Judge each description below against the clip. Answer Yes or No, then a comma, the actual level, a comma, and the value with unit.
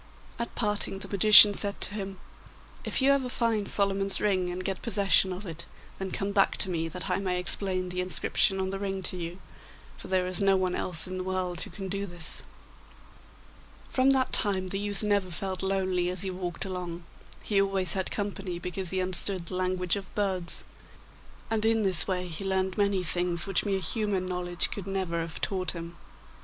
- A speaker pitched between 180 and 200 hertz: Yes, high, 190 Hz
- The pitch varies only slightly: Yes, narrow, 1.7 semitones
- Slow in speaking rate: No, average, 195 wpm